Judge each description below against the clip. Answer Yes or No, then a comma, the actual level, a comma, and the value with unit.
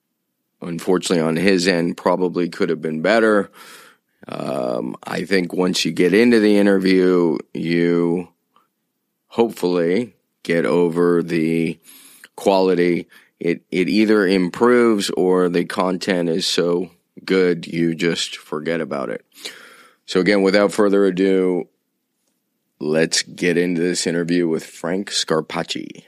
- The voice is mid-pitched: No, very low, 90 Hz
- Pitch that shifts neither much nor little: No, narrow, 2.2 semitones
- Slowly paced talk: Yes, slow, 120 wpm